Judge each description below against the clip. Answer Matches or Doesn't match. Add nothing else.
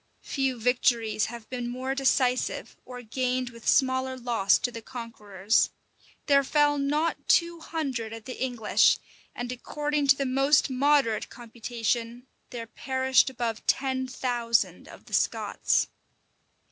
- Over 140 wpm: Doesn't match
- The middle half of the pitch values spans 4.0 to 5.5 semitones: Doesn't match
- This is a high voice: Matches